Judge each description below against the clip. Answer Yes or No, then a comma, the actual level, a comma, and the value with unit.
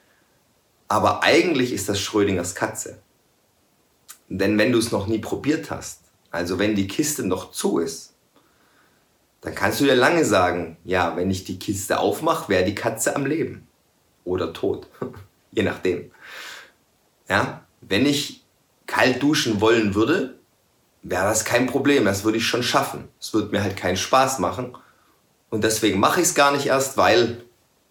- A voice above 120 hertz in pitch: No, low, 110 Hz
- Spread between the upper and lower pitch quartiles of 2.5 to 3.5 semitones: No, average, 4.9 semitones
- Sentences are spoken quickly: No, average, 160 wpm